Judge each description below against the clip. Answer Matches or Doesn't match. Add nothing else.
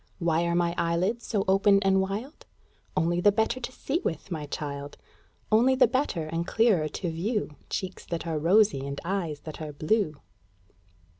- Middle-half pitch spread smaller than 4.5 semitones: Doesn't match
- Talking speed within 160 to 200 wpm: Matches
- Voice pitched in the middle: Matches